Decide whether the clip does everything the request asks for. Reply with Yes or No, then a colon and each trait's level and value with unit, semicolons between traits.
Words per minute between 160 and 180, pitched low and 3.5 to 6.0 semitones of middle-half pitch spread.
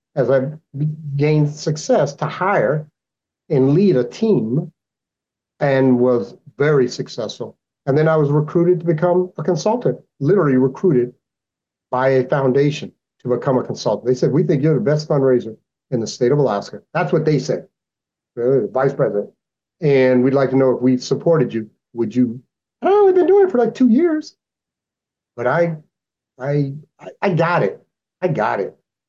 No: average, 170 wpm; medium, 145 Hz; average, 4.9 semitones